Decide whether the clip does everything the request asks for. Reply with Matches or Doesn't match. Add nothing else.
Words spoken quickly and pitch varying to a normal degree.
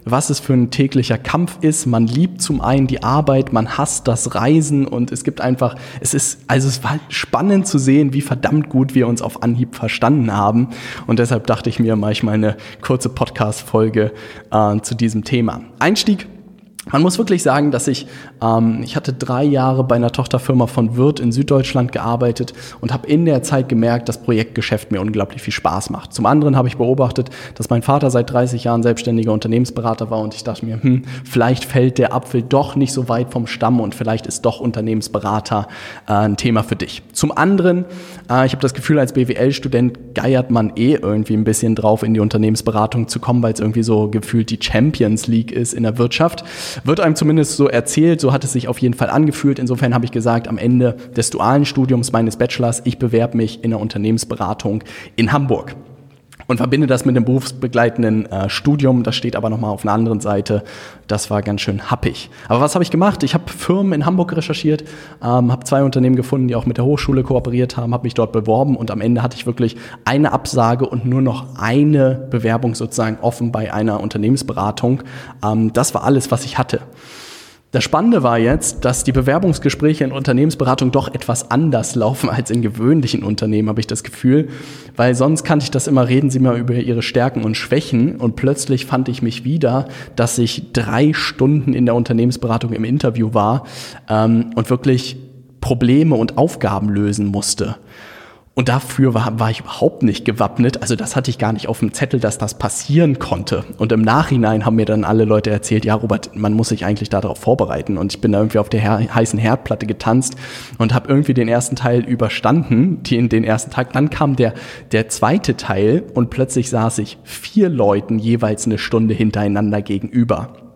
Matches